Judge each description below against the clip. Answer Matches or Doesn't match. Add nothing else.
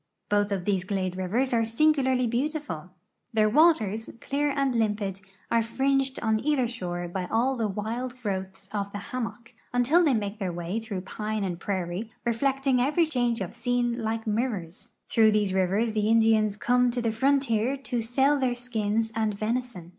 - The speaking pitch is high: Matches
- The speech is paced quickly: Doesn't match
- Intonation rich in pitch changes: Doesn't match